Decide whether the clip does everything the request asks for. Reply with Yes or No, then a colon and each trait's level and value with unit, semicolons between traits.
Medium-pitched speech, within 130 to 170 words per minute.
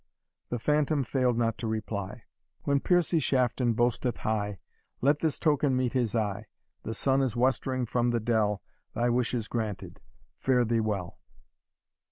No: low, 120 Hz; average, 155 wpm